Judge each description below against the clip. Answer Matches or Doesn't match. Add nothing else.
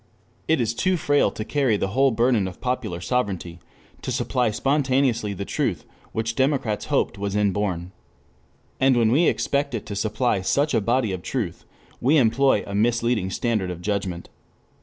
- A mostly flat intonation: Doesn't match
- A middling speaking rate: Matches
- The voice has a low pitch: Matches